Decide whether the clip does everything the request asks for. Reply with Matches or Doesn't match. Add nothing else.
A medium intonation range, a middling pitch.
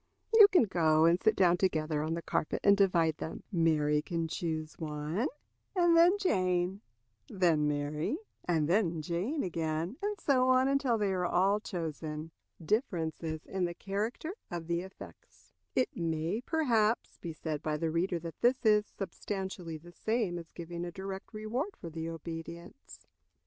Matches